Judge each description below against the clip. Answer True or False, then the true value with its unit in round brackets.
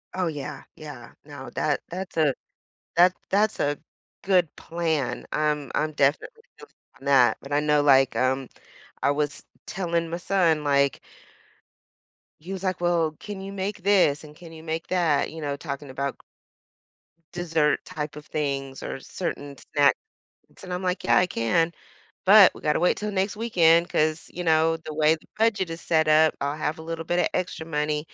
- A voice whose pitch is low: False (160 Hz)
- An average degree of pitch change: True (3.4 semitones)